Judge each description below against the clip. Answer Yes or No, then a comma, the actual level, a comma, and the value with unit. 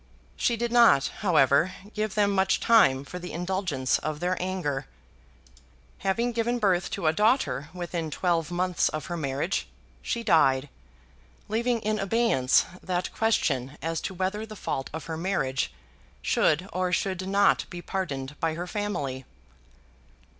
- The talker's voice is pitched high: No, medium, 180 Hz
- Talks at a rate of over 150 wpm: No, average, 145 wpm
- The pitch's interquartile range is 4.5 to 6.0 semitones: Yes, average, 5.2 semitones